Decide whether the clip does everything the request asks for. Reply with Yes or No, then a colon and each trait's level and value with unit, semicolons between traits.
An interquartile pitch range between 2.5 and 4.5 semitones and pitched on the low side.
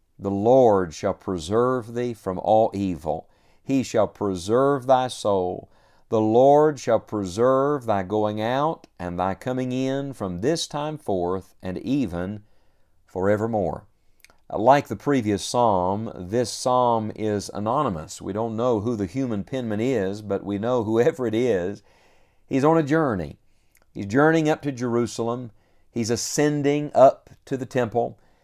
No: average, 4.9 semitones; low, 110 Hz